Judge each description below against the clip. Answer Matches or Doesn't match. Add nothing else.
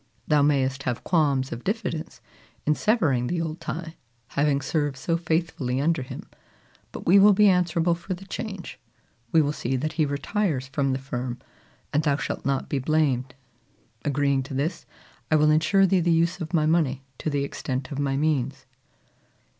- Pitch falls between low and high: Matches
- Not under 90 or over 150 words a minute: Doesn't match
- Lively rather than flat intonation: Doesn't match